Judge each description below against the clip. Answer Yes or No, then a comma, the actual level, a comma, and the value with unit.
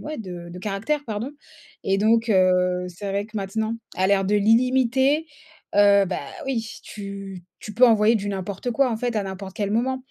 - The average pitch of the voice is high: Yes, high, 205 Hz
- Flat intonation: No, average, 3.1 semitones